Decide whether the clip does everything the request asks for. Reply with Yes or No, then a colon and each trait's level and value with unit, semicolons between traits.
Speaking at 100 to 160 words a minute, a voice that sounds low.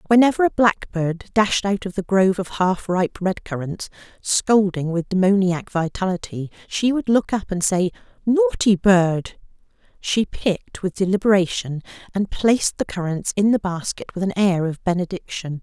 No: average, 155 wpm; high, 190 Hz